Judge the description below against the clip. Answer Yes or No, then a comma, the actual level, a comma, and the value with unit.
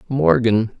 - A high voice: No, low, 115 Hz